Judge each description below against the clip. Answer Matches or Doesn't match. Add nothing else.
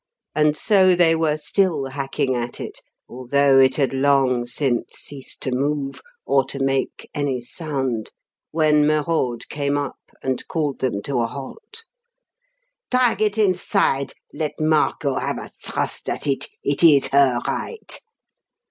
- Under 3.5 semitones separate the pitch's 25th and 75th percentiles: Matches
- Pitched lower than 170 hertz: Matches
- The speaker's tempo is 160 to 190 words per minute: Doesn't match